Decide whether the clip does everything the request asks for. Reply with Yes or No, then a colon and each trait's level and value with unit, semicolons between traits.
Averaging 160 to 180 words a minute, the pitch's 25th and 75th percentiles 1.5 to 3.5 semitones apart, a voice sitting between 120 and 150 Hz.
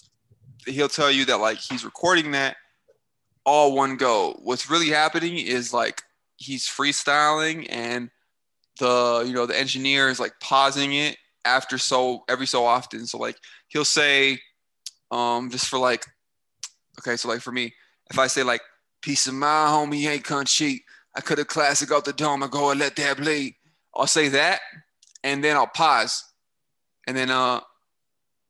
Yes: average, 170 wpm; average, 2.9 semitones; low, 135 Hz